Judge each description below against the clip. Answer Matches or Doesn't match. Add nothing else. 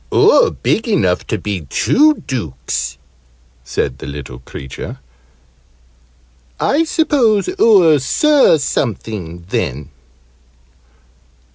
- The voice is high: Doesn't match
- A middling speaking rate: Doesn't match